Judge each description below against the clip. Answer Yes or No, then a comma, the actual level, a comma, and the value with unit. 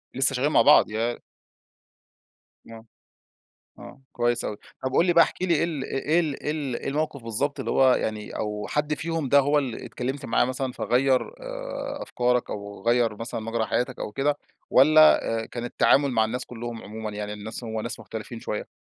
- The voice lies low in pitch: Yes, low, 125 Hz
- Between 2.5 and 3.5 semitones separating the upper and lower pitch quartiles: No, average, 4.5 semitones